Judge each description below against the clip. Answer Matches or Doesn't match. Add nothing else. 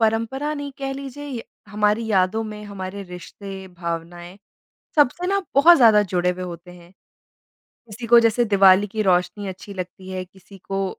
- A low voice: Doesn't match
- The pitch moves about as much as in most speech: Matches